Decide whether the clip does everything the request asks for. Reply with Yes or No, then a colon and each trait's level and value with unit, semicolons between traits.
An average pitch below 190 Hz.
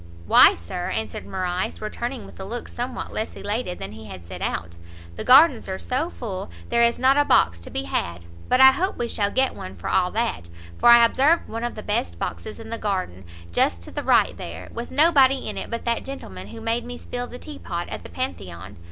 No: high, 225 Hz